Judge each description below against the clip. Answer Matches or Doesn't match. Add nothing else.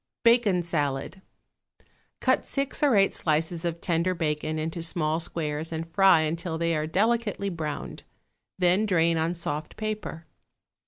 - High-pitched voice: Doesn't match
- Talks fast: Doesn't match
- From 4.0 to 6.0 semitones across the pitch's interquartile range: Doesn't match